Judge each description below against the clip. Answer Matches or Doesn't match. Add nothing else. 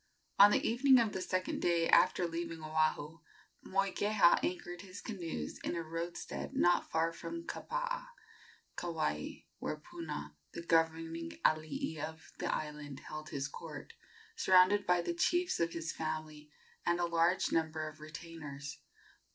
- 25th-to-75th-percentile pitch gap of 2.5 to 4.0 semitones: Matches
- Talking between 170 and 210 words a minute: Doesn't match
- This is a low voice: Doesn't match